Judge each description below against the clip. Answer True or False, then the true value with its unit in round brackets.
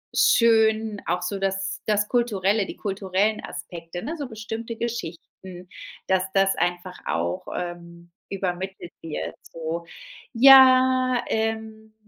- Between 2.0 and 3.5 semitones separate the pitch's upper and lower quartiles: False (4.0 semitones)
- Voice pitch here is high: True (195 Hz)